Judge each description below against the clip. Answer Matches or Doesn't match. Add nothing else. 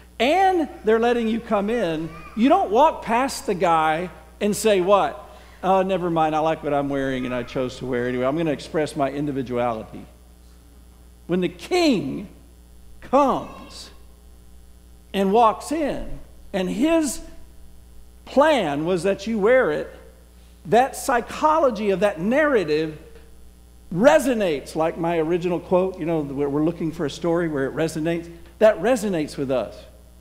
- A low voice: Doesn't match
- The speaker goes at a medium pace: Matches